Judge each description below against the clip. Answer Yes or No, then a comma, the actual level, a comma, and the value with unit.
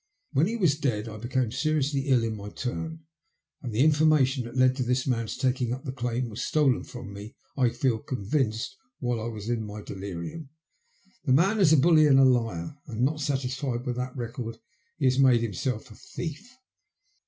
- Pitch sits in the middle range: No, low, 125 Hz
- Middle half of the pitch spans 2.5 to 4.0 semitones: Yes, average, 3.7 semitones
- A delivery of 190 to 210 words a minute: Yes, average, 195 wpm